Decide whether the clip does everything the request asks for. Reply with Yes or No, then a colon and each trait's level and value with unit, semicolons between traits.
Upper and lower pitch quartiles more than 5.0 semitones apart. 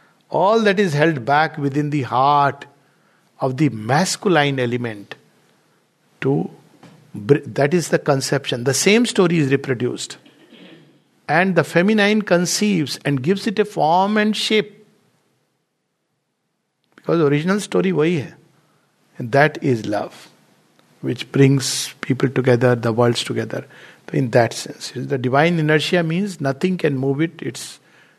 Yes: wide, 5.4 semitones